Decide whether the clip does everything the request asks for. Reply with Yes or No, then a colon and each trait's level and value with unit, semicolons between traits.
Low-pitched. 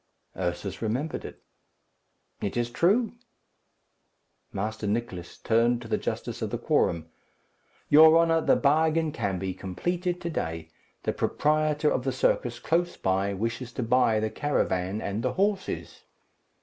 Yes: low, 120 Hz